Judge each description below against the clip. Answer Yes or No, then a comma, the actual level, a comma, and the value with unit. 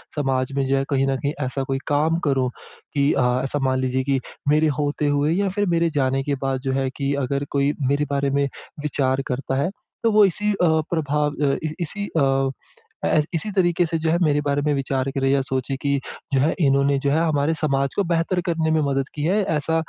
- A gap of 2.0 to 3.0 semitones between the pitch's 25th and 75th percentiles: Yes, average, 2.7 semitones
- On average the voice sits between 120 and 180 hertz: Yes, medium, 140 Hz